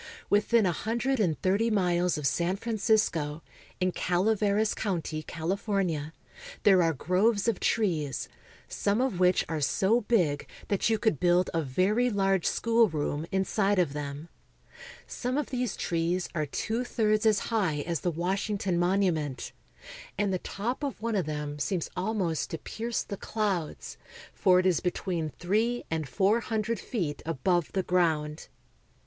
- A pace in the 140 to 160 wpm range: Yes, average, 145 wpm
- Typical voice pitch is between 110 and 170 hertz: No, medium, 185 Hz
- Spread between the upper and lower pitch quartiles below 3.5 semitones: No, average, 4.7 semitones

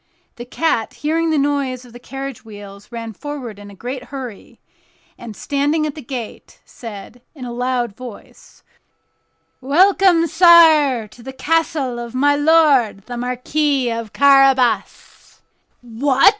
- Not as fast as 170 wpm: Yes, average, 140 wpm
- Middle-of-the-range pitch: No, very high, 260 Hz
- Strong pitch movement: No, average, 3.6 semitones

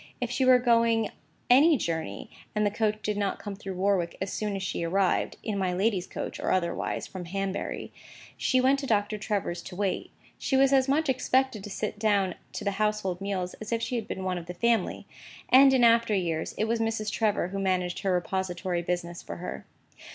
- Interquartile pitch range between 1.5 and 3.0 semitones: No, average, 3.8 semitones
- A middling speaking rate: No, fast, 210 wpm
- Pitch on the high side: Yes, high, 205 Hz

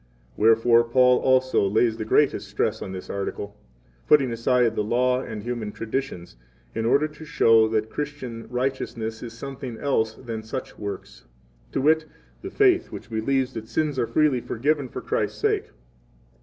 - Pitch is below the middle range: Yes, low, 120 Hz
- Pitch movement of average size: Yes, average, 3.4 semitones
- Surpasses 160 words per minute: Yes, average, 170 wpm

